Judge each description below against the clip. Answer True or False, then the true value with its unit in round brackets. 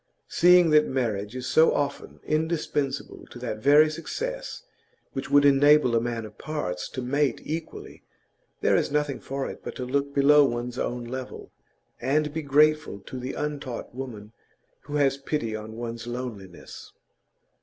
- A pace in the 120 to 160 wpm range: True (155 wpm)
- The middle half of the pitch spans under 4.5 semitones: True (3.7 semitones)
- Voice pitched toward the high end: False (135 Hz)